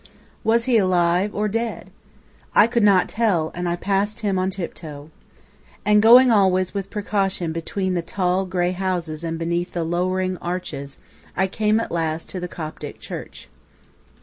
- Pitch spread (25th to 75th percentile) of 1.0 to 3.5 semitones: Yes, average, 3.1 semitones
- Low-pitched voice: No, medium, 185 Hz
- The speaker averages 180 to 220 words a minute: No, average, 160 wpm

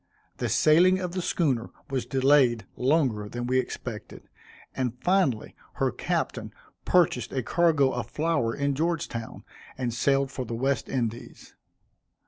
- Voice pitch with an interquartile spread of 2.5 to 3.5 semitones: No, average, 4.5 semitones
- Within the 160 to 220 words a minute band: No, slow, 135 wpm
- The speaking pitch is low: Yes, low, 130 Hz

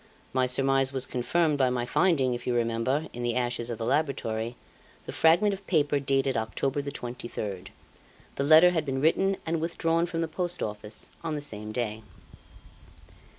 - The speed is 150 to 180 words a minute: Yes, average, 175 wpm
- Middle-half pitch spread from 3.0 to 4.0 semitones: No, average, 4.9 semitones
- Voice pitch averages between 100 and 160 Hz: Yes, low, 135 Hz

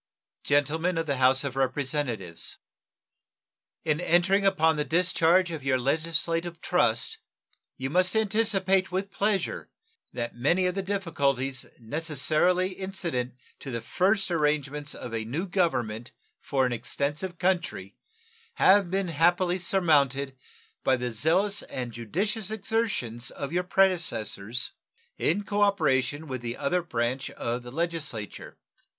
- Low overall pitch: No, medium, 160 Hz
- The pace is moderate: No, slow, 125 wpm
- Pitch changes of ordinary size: No, wide, 5.9 semitones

